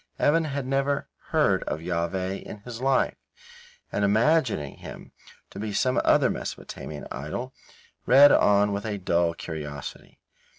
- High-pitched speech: No, low, 105 Hz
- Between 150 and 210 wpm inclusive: No, slow, 135 wpm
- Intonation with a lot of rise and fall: Yes, wide, 7.6 semitones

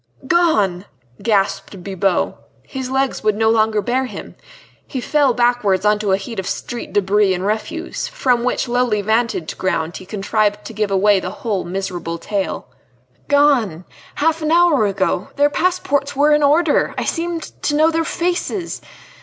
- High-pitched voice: Yes, high, 220 Hz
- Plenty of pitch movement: Yes, wide, 6.6 semitones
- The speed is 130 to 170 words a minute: Yes, average, 160 wpm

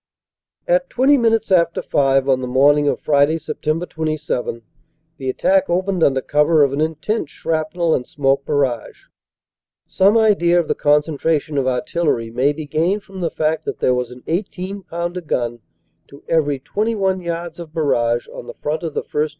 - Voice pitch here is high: No, medium, 155 Hz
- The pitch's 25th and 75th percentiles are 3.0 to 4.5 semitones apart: Yes, average, 4.0 semitones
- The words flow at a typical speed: Yes, average, 175 wpm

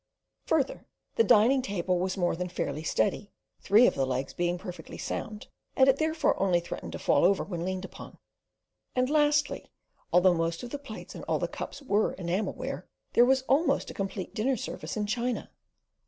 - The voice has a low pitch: No, high, 205 Hz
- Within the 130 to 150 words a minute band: No, average, 185 wpm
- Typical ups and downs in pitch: No, wide, 6.5 semitones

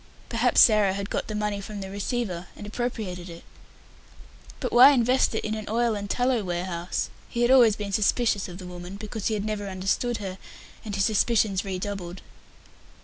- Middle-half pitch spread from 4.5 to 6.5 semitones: No, average, 3.3 semitones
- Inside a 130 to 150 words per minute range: No, average, 185 wpm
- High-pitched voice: Yes, high, 205 Hz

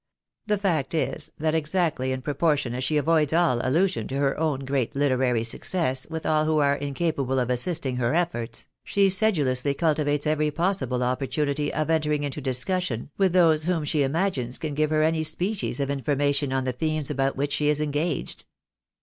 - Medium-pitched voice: Yes, medium, 150 Hz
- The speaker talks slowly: No, average, 180 wpm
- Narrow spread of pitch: No, average, 3.3 semitones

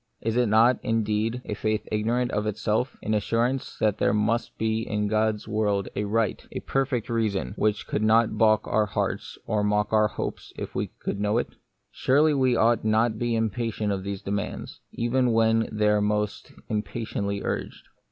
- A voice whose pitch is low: Yes, low, 110 Hz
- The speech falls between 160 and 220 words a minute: Yes, average, 185 wpm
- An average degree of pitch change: No, narrow, 1.7 semitones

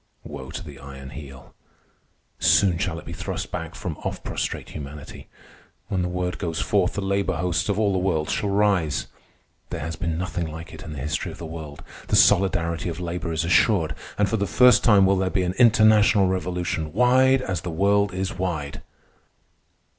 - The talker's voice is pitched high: No, very low, 90 Hz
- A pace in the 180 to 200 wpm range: Yes, average, 190 wpm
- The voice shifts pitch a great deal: No, average, 3.8 semitones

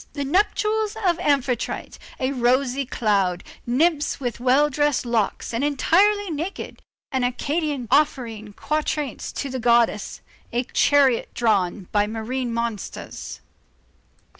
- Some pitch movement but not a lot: Yes, average, 4.1 semitones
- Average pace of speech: No, slow, 115 wpm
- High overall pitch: Yes, very high, 260 Hz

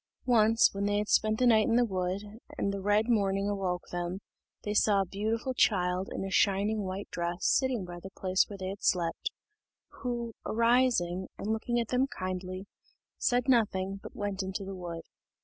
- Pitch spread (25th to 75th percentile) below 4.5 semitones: Yes, average, 3.1 semitones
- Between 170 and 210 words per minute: Yes, average, 185 wpm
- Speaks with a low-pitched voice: No, high, 200 Hz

